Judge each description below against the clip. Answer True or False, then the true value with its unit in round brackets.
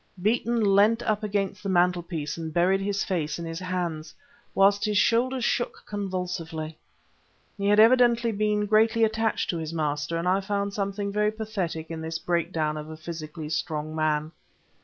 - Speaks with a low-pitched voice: False (185 Hz)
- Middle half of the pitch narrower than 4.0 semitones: False (4.5 semitones)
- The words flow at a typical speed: True (165 wpm)